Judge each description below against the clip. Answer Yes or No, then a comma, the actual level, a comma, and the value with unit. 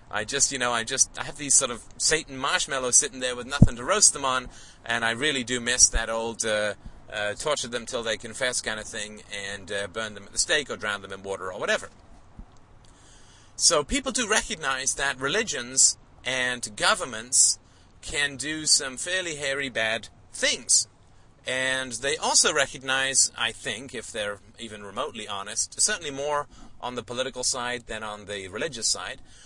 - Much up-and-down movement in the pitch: No, average, 4.1 semitones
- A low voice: Yes, low, 120 Hz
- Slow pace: No, average, 180 wpm